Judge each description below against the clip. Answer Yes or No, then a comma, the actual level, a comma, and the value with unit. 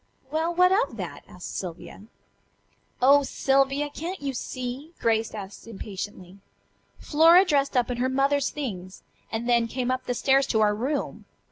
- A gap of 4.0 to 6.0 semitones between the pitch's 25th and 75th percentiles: Yes, average, 4.4 semitones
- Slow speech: No, average, 155 wpm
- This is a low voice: No, very high, 260 Hz